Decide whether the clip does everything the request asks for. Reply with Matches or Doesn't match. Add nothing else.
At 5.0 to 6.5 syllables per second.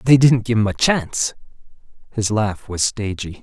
Doesn't match